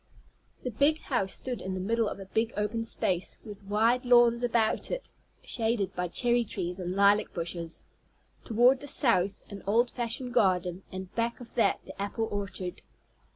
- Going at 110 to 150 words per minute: No, average, 170 wpm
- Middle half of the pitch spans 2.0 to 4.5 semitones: Yes, average, 3.9 semitones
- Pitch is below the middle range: No, high, 220 Hz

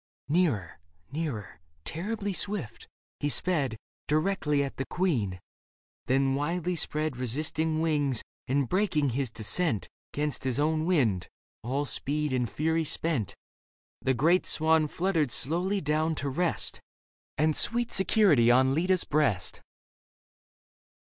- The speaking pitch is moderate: Yes, medium, 150 Hz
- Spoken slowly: Yes, slow, 125 wpm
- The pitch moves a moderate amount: Yes, average, 4.1 semitones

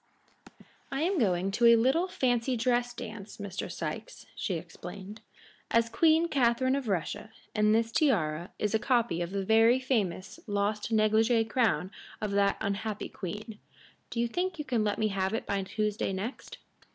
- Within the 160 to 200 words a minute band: Yes, average, 165 wpm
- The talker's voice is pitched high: Yes, high, 220 Hz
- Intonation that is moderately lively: Yes, average, 3.4 semitones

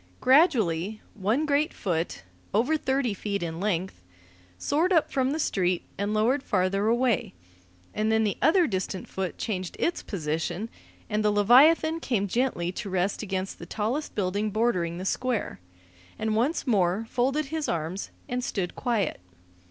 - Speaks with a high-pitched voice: Yes, high, 215 Hz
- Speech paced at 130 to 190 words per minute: Yes, average, 150 wpm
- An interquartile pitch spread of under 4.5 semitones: No, wide, 5.5 semitones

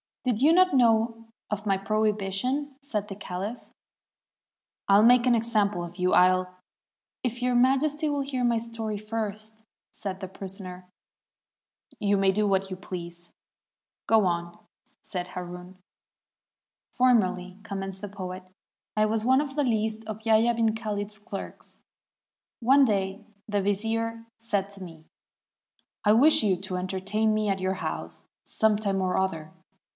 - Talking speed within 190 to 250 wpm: No, average, 150 wpm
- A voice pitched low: No, high, 210 Hz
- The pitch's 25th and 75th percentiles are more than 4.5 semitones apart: No, average, 3.1 semitones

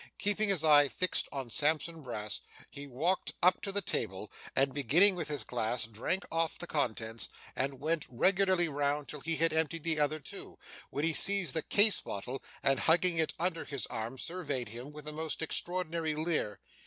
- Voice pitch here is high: No, medium, 155 Hz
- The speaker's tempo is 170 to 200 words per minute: Yes, average, 185 wpm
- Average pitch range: Yes, average, 4.0 semitones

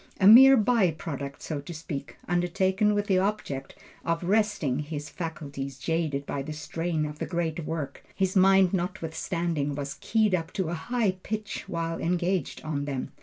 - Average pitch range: Yes, average, 4.1 semitones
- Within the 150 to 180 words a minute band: Yes, average, 170 wpm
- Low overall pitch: No, medium, 170 Hz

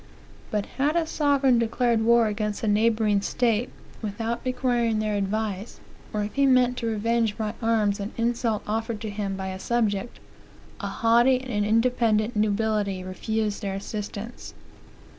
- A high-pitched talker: Yes, high, 220 Hz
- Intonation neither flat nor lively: No, narrow, 2.3 semitones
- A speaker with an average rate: Yes, average, 150 wpm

